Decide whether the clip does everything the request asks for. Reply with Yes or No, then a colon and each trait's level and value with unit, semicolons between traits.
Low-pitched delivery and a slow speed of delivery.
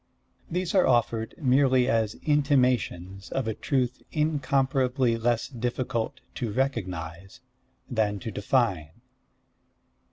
Yes: low, 125 Hz; slow, 100 wpm